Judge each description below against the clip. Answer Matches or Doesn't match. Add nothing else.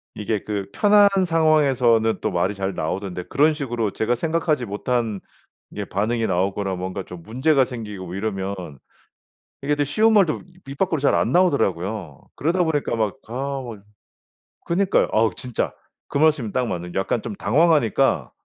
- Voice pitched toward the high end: Doesn't match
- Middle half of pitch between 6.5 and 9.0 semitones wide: Matches